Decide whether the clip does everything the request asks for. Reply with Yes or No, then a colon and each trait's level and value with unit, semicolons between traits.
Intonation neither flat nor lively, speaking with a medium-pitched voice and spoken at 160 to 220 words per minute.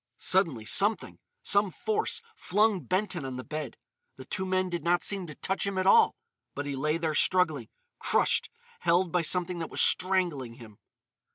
Yes: average, 4.2 semitones; medium, 180 Hz; average, 165 wpm